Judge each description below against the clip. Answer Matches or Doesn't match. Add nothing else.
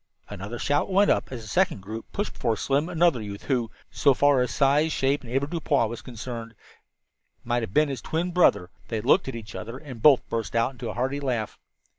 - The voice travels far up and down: Doesn't match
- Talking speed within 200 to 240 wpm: Matches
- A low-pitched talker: Matches